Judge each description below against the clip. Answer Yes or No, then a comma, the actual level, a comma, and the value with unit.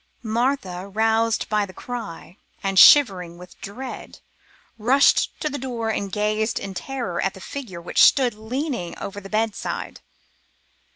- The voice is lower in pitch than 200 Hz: No, high, 215 Hz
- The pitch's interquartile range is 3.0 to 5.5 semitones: Yes, average, 4.2 semitones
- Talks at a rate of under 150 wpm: Yes, average, 140 wpm